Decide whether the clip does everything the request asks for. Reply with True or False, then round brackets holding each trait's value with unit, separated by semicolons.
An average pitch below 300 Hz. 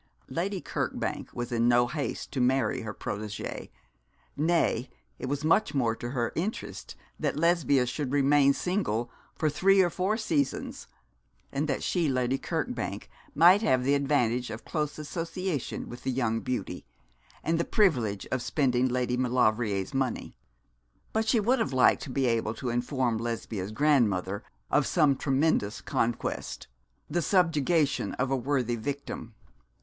True (135 Hz)